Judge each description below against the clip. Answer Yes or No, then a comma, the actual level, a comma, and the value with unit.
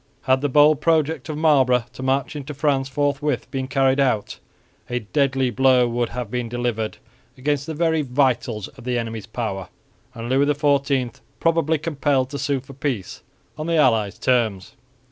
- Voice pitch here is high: No, low, 135 Hz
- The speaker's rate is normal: Yes, average, 165 wpm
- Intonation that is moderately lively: Yes, average, 3.1 semitones